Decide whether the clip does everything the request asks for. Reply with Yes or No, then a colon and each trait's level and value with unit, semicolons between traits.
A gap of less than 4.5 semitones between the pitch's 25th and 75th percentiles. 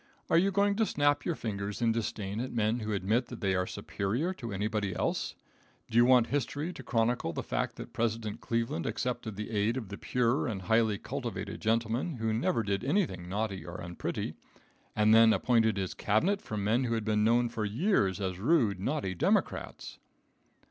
Yes: average, 3.4 semitones